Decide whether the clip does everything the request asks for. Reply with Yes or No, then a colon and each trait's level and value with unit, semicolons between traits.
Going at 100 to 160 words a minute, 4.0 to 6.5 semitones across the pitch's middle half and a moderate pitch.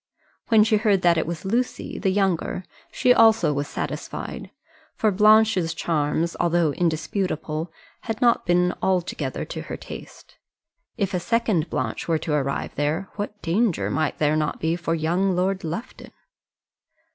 Yes: average, 150 wpm; average, 4.4 semitones; medium, 180 Hz